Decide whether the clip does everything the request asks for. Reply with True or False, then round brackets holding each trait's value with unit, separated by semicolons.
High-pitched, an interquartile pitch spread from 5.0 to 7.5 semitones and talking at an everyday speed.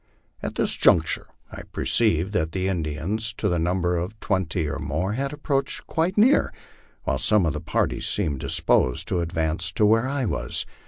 False (90 Hz; 5.3 semitones; 175 wpm)